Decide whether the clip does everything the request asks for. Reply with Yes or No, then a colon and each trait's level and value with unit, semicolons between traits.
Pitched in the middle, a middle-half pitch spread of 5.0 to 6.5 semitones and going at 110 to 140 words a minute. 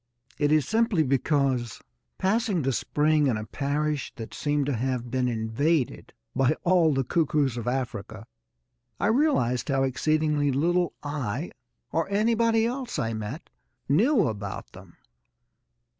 Yes: medium, 145 Hz; wide, 5.4 semitones; slow, 135 wpm